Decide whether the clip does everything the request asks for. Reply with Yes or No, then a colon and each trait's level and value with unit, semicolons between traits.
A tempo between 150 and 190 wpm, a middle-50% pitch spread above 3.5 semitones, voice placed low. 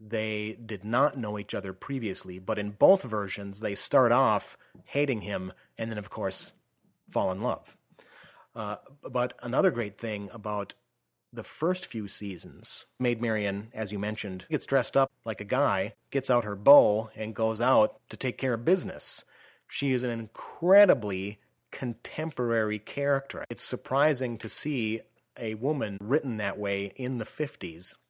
Yes: average, 160 wpm; average, 4.0 semitones; low, 110 Hz